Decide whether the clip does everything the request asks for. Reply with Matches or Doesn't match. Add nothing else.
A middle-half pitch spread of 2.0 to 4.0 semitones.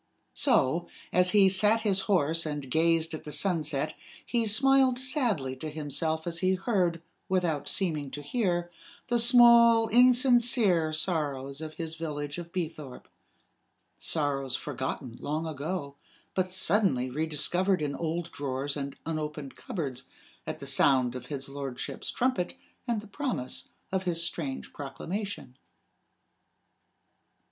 Doesn't match